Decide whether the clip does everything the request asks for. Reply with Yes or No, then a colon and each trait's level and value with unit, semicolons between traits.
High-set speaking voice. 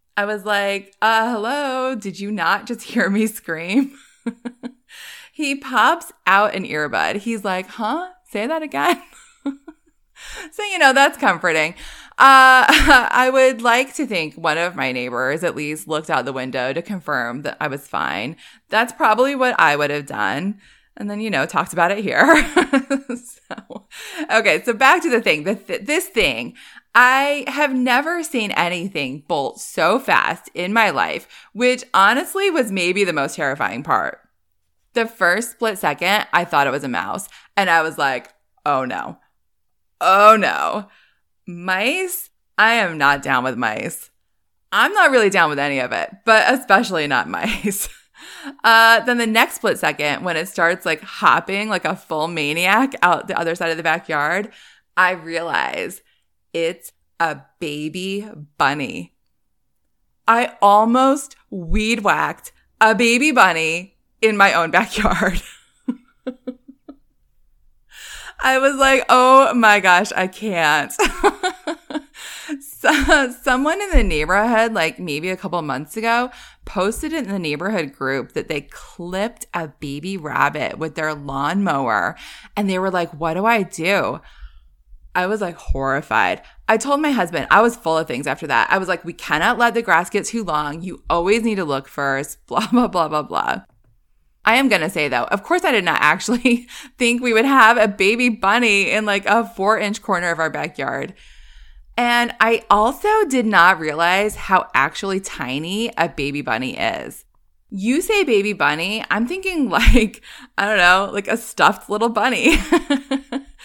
Yes: high, 210 Hz